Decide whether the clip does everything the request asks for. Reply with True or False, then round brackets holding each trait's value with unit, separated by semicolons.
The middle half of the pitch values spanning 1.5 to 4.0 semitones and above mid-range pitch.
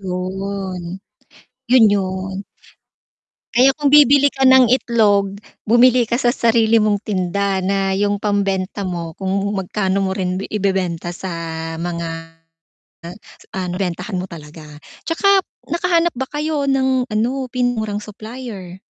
False (4.7 semitones; 200 Hz)